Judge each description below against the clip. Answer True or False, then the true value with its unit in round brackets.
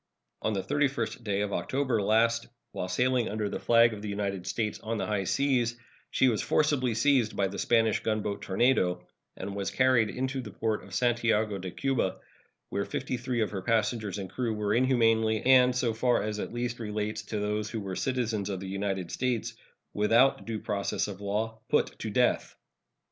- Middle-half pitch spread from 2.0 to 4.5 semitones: True (3.0 semitones)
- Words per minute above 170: True (190 wpm)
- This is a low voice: True (110 Hz)